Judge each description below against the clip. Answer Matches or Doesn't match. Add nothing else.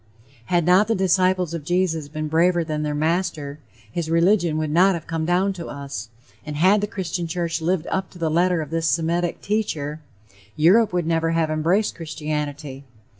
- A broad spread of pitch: Doesn't match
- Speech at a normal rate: Matches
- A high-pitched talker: Doesn't match